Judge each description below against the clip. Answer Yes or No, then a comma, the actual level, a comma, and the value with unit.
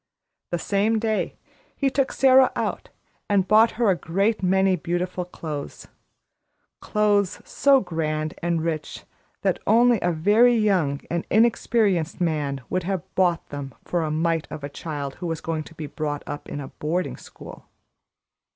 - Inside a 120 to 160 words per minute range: Yes, average, 155 wpm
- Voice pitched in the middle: Yes, medium, 175 Hz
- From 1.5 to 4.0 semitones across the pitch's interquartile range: No, average, 5.1 semitones